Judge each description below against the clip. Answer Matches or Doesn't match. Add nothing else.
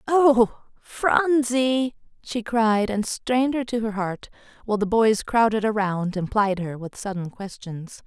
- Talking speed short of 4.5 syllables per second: Matches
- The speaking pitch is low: Doesn't match